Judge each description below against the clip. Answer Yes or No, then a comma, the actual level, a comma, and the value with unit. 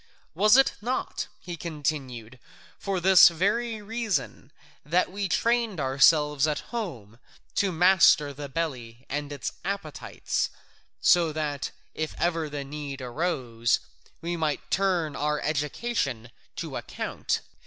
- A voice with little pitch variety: No, average, 5.1 semitones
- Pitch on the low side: No, medium, 155 Hz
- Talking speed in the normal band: No, slow, 120 wpm